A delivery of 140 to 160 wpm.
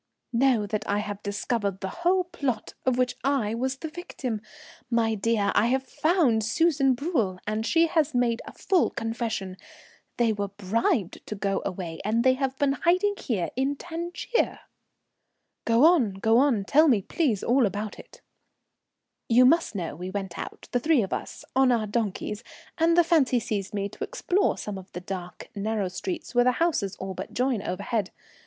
No: average, 180 wpm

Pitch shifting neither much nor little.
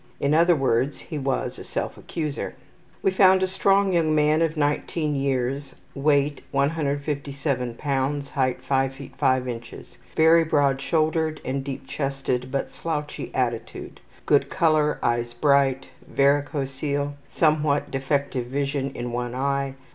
No: narrow, 2.3 semitones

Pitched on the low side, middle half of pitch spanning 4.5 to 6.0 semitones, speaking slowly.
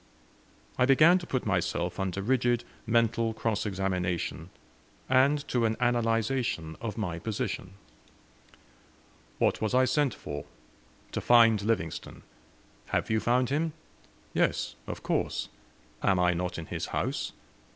Yes: low, 115 Hz; average, 5.1 semitones; slow, 130 wpm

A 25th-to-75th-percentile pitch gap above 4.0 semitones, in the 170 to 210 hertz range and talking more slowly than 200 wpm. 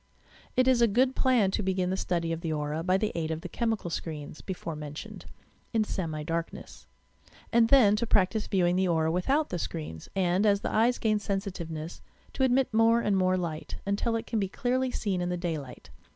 No: average, 5.2 semitones; high, 190 Hz; fast, 205 wpm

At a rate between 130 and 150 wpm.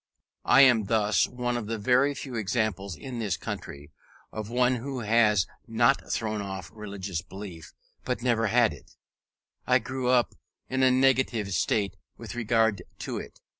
No: average, 160 wpm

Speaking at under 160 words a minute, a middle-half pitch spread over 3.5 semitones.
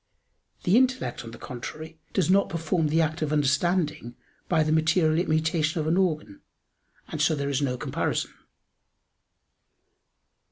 No: average, 145 wpm; narrow, 2.4 semitones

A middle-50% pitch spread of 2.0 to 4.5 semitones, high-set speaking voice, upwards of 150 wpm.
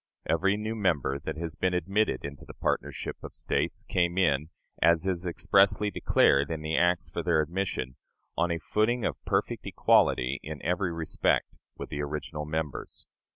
No: average, 3.8 semitones; very low, 85 Hz; average, 165 wpm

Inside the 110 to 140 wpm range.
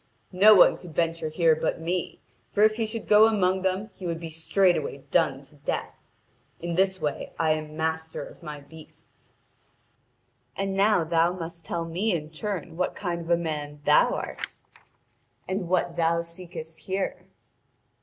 No: average, 165 wpm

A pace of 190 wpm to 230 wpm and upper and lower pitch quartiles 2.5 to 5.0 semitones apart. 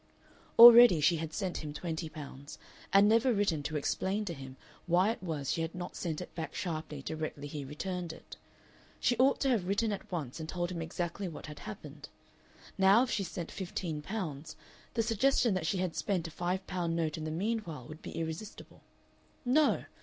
Yes: average, 195 wpm; average, 4.3 semitones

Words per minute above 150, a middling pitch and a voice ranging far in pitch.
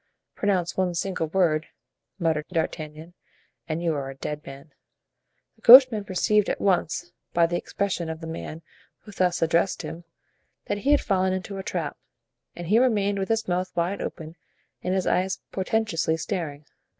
No: average, 165 wpm; medium, 180 Hz; average, 3.4 semitones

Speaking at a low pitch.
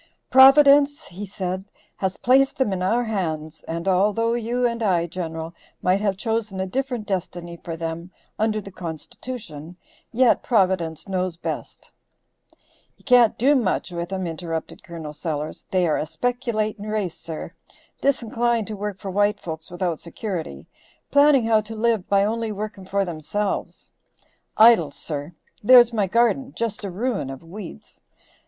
No: high, 200 Hz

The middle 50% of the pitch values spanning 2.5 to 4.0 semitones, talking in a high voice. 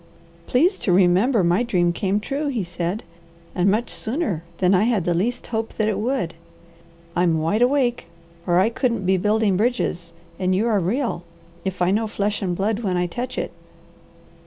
No: average, 4.7 semitones; high, 205 Hz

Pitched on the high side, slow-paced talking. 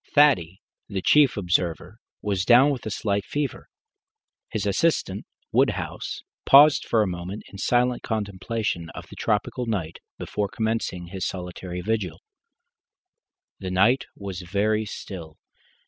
No: low, 100 Hz; slow, 130 wpm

